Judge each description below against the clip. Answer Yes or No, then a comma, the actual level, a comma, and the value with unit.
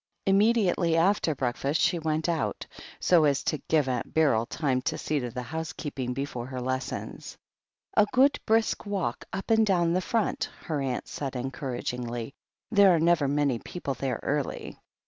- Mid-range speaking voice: Yes, medium, 150 Hz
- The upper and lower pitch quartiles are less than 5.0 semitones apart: No, wide, 5.4 semitones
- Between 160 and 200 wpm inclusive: Yes, average, 165 wpm